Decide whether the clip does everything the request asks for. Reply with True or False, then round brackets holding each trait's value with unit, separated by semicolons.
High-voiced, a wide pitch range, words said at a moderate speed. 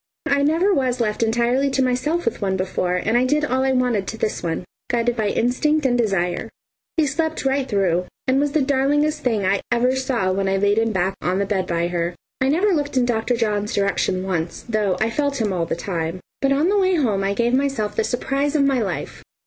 False (240 Hz; 5.8 semitones; 230 wpm)